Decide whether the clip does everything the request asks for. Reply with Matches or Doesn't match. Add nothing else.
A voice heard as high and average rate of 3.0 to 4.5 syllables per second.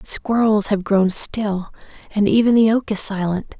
Matches